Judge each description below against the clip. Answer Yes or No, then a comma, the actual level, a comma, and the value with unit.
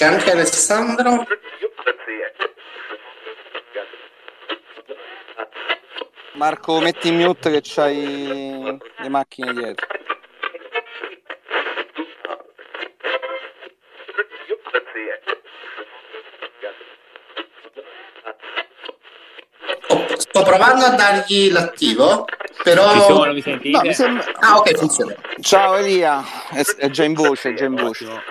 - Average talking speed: No, slow, 70 wpm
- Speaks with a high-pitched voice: Yes, high, 210 Hz